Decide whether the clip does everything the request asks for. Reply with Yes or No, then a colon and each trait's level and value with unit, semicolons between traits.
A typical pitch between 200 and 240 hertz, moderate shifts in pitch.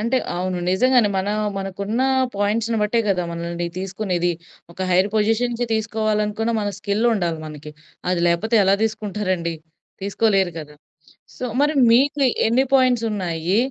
Yes: high, 205 Hz; average, 3.8 semitones